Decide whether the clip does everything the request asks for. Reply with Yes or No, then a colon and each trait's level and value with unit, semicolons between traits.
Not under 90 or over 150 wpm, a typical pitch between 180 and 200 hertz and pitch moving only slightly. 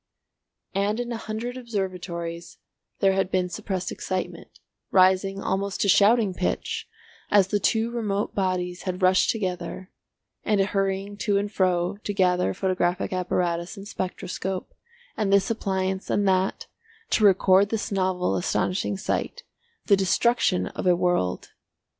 Yes: average, 140 wpm; high, 190 Hz; narrow, 1.8 semitones